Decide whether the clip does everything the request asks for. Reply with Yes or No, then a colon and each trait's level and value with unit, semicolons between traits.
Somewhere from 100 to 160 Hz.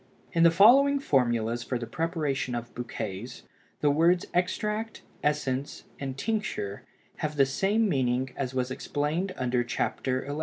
Yes: medium, 140 Hz